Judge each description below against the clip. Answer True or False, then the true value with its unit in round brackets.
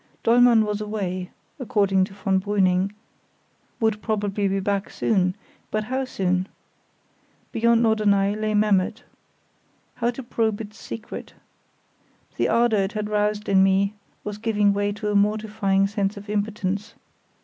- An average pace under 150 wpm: True (140 wpm)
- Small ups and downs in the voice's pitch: True (1.9 semitones)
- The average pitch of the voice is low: False (210 Hz)